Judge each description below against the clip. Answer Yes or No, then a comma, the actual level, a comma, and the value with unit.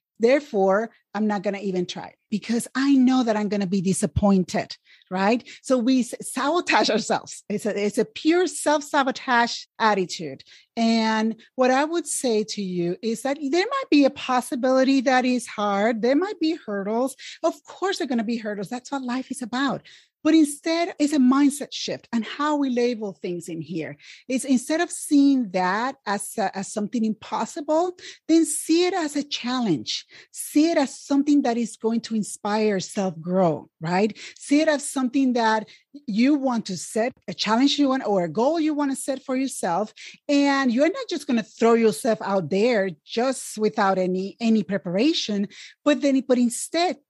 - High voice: Yes, high, 245 Hz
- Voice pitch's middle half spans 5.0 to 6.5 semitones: Yes, wide, 5.4 semitones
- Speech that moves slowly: No, average, 185 wpm